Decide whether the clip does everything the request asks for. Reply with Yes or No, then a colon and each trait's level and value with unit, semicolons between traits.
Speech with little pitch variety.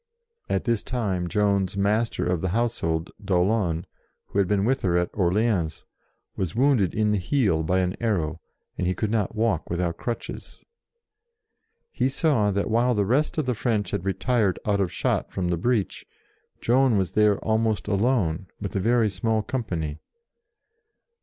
No: average, 4.2 semitones